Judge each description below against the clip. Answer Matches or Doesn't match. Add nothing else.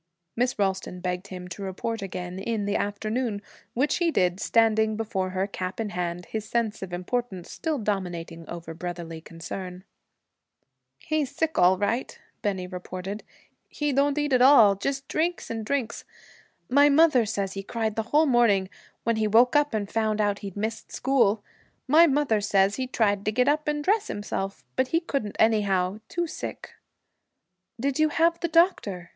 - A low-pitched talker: Doesn't match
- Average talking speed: Matches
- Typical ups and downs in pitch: Doesn't match